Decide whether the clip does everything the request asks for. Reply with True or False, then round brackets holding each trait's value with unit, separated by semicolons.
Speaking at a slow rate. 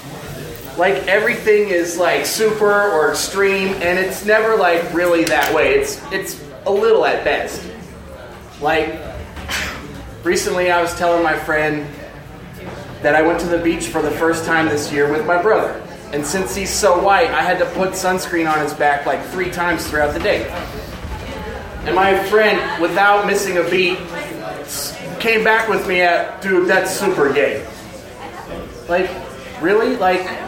False (160 wpm)